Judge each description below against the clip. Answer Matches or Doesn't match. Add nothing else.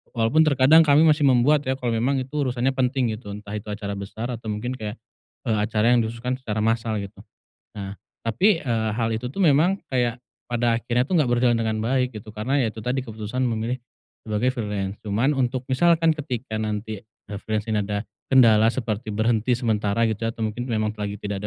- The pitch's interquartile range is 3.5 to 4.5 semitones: Doesn't match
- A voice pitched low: Matches